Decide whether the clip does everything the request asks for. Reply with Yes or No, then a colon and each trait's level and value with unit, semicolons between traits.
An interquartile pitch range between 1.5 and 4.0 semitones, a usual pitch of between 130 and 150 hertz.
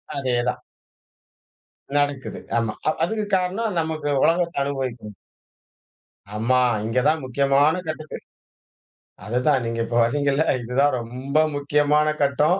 Yes: average, 3.6 semitones; medium, 140 Hz